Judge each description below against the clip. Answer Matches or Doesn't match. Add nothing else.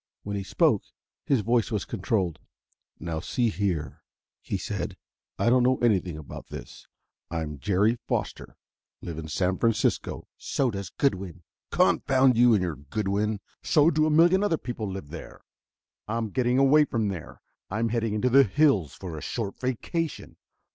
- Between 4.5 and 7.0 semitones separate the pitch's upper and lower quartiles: Matches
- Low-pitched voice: Matches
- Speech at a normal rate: Matches